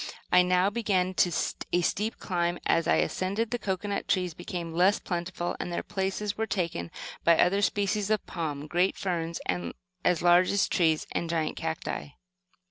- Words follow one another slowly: No, average, 160 wpm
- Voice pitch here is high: No, medium, 180 Hz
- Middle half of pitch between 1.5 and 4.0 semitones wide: Yes, average, 2.7 semitones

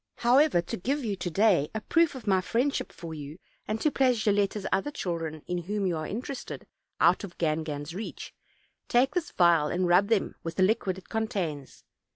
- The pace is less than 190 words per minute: No, average, 195 wpm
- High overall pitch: Yes, high, 195 Hz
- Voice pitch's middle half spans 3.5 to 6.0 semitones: Yes, wide, 5.4 semitones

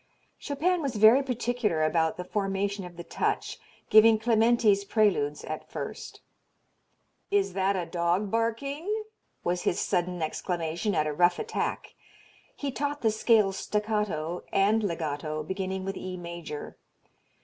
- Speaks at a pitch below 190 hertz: No, high, 195 Hz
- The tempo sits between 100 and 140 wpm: Yes, slow, 135 wpm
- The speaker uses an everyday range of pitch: Yes, average, 4.7 semitones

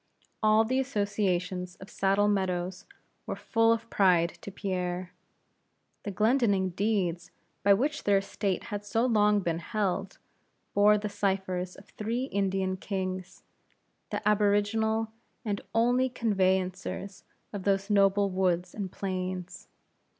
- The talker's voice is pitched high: Yes, high, 200 Hz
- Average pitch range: No, narrow, 2.2 semitones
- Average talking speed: No, slow, 125 wpm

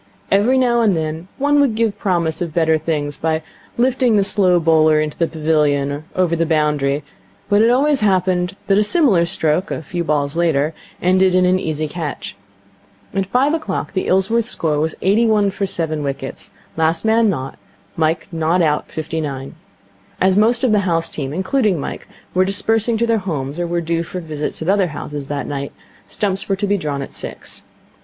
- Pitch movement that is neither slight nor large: Yes, average, 4.7 semitones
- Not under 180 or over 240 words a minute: Yes, average, 195 wpm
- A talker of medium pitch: Yes, medium, 175 Hz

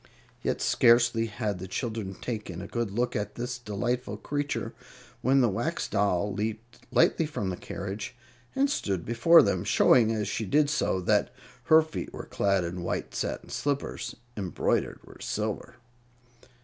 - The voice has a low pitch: Yes, low, 110 Hz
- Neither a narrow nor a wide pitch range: Yes, average, 3.8 semitones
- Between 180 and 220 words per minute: No, average, 155 wpm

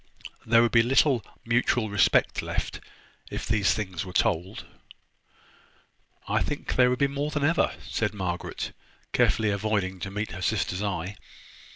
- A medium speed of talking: Yes, average, 150 wpm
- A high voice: No, low, 105 Hz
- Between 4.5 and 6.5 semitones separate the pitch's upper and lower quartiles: No, average, 3.8 semitones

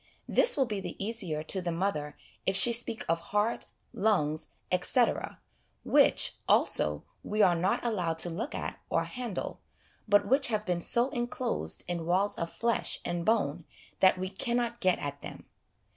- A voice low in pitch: No, high, 195 Hz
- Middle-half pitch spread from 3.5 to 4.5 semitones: No, average, 5.3 semitones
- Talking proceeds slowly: No, average, 165 wpm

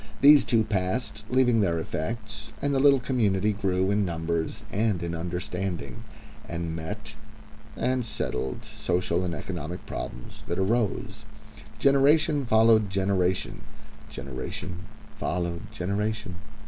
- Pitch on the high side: No, very low, 95 Hz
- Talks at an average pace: No, slow, 115 wpm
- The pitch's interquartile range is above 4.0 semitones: Yes, average, 4.5 semitones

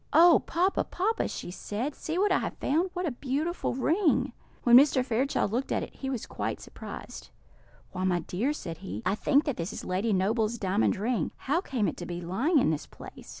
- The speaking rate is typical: No, fast, 210 wpm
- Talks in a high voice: Yes, very high, 250 Hz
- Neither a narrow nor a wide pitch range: No, wide, 8.2 semitones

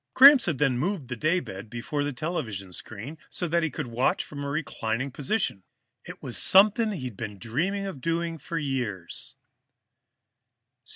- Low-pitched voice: No, medium, 145 Hz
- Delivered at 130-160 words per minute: Yes, average, 155 wpm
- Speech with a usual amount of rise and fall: No, wide, 6.2 semitones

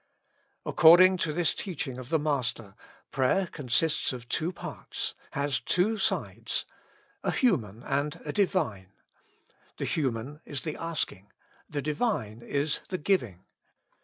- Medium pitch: Yes, medium, 145 Hz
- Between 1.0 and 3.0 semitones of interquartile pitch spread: No, wide, 5.6 semitones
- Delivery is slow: Yes, slow, 130 wpm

